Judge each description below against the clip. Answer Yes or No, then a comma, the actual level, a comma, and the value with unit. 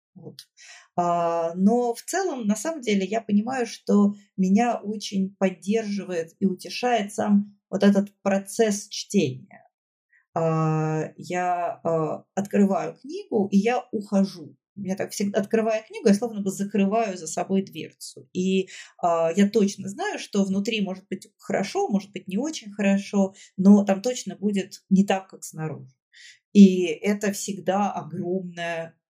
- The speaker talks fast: No, average, 130 wpm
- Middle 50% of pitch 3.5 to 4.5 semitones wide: No, average, 2.7 semitones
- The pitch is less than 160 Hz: No, high, 195 Hz